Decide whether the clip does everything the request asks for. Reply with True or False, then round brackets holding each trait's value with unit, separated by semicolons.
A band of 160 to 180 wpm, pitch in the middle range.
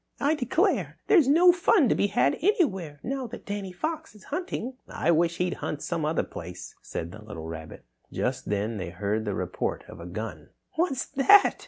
False (190 wpm; 180 Hz)